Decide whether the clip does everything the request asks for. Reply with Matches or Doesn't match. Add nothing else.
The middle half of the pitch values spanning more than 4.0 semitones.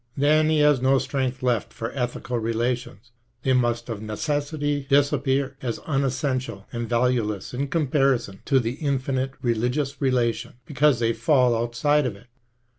Doesn't match